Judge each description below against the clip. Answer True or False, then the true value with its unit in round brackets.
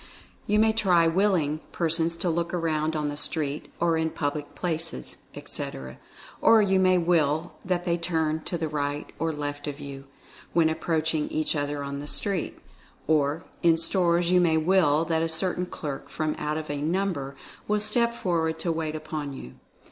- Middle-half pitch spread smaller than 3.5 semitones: True (2.8 semitones)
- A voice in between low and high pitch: True (160 Hz)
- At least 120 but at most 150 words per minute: False (180 wpm)